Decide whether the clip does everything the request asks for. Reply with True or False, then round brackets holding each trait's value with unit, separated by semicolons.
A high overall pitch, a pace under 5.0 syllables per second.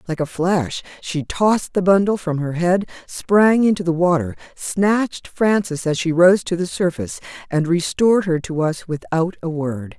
False (175 Hz; 4.6 syllables/s)